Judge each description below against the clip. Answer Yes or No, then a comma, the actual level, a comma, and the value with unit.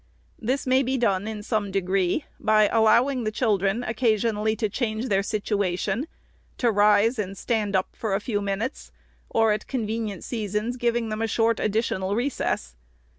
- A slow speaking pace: No, average, 160 wpm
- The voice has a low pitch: No, high, 215 Hz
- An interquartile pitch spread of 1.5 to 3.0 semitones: Yes, narrow, 2.5 semitones